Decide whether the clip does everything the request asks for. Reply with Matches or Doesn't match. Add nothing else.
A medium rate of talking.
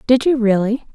Matches